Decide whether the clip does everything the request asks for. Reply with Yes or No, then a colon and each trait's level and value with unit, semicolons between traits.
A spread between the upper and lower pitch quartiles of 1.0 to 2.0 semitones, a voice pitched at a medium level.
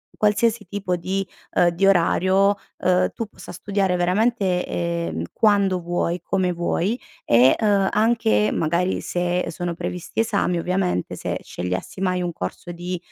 No: narrow, 2.4 semitones; medium, 180 Hz